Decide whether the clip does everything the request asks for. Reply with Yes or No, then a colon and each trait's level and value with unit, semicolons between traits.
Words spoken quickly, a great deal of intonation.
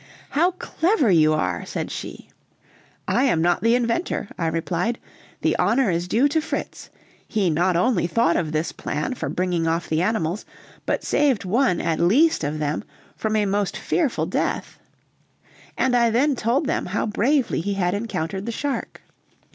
No: average, 170 wpm; wide, 6.7 semitones